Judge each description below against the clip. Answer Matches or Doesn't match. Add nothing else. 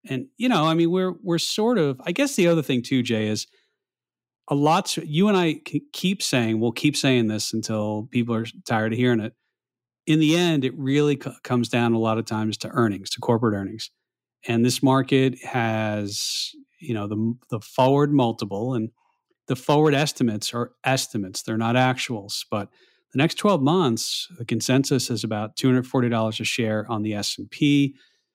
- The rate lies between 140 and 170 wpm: Doesn't match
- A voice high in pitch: Doesn't match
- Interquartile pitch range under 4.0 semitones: Doesn't match